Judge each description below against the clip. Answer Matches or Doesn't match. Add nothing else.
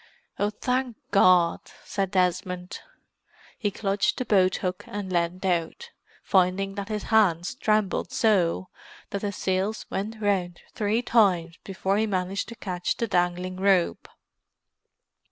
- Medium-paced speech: Doesn't match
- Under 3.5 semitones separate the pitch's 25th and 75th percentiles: Matches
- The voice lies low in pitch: Doesn't match